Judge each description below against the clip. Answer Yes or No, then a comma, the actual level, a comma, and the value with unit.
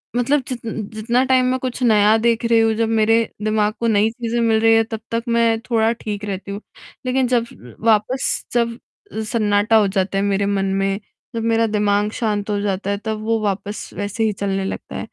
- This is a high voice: Yes, high, 220 Hz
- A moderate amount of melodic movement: No, narrow, 2.3 semitones